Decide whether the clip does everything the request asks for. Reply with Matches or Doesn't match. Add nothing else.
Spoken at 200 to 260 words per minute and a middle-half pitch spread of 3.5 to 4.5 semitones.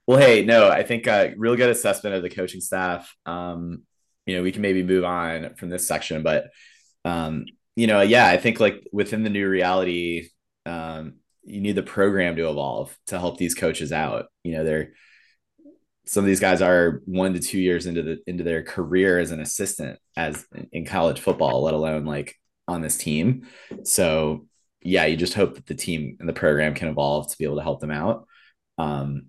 Doesn't match